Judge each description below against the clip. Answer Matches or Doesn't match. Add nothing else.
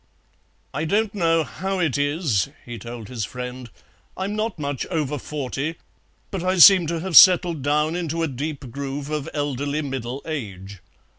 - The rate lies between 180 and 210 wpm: Doesn't match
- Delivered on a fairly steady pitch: Doesn't match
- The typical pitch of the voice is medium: Matches